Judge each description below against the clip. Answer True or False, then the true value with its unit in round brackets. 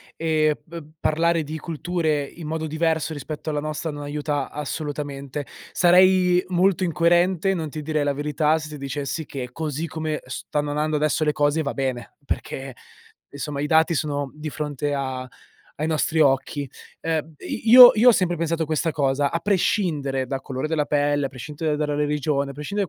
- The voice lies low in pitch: False (150 Hz)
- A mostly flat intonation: True (2.2 semitones)